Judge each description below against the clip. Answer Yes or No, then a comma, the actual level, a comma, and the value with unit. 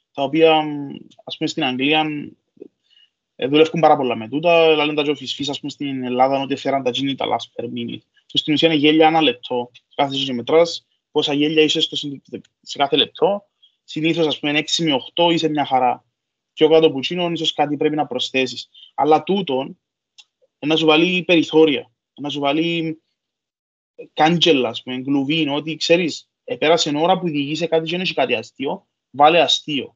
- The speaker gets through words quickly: Yes, fast, 175 wpm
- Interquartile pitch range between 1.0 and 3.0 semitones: Yes, average, 2.7 semitones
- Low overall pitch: No, medium, 155 Hz